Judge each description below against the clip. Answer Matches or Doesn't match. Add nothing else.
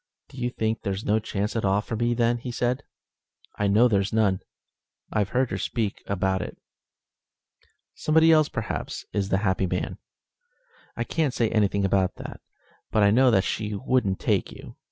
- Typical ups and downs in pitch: Matches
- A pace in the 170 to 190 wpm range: Matches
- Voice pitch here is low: Matches